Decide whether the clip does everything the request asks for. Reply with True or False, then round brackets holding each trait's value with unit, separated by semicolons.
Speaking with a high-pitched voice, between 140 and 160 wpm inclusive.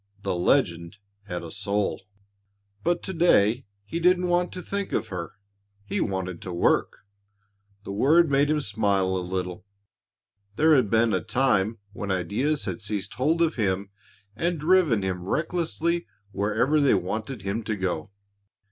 False (110 Hz; 155 wpm)